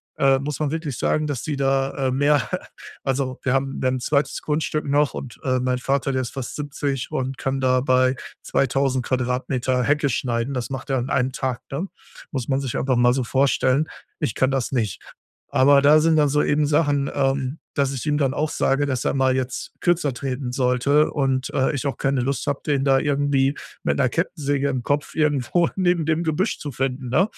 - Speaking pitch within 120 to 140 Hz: Yes, low, 135 Hz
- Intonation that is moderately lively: No, narrow, 2.0 semitones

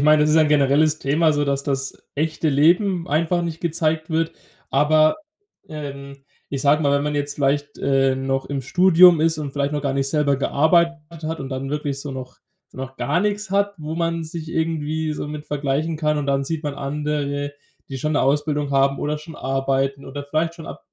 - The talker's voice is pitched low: No, medium, 150 Hz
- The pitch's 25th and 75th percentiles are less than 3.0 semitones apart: Yes, narrow, 2.4 semitones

